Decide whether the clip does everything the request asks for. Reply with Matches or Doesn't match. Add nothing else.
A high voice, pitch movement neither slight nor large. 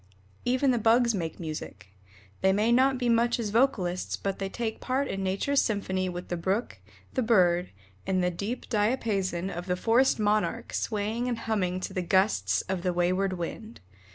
Matches